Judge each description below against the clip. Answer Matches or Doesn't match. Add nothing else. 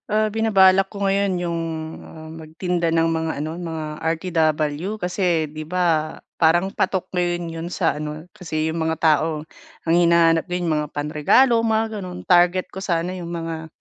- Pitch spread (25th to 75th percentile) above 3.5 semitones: Doesn't match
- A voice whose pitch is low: Doesn't match